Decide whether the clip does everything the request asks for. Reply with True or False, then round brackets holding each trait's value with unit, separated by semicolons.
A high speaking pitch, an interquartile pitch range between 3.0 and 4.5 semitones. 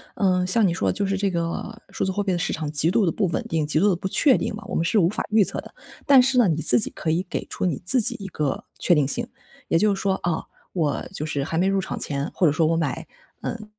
False (180 Hz; 4.2 semitones)